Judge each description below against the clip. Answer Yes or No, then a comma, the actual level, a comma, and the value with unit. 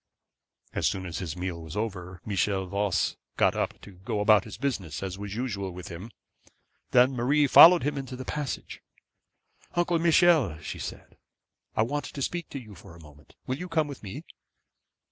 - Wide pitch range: Yes, wide, 7.0 semitones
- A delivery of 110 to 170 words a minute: No, average, 185 wpm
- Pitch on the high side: No, low, 105 Hz